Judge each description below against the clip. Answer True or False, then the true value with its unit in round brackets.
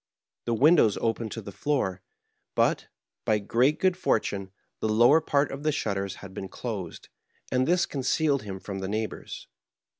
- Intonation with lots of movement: True (6.1 semitones)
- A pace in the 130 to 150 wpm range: False (160 wpm)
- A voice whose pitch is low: True (115 Hz)